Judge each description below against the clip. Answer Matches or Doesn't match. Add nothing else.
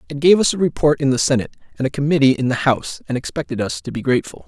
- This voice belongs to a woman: Doesn't match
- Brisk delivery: Matches